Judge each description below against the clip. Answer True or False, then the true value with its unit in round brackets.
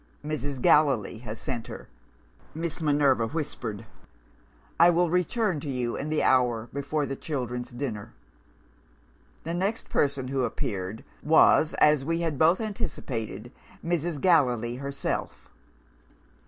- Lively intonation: False (4.9 semitones)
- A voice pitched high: False (140 Hz)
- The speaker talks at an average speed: False (125 wpm)